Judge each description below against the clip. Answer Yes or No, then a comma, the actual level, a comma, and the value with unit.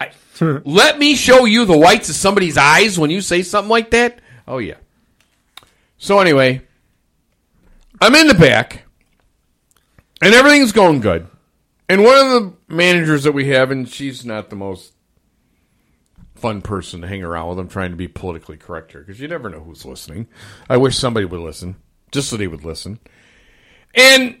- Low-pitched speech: Yes, low, 130 Hz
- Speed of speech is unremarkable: Yes, average, 175 wpm